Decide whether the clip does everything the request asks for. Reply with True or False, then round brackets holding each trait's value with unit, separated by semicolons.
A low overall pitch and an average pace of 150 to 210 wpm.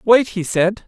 False (200 Hz; 205 wpm)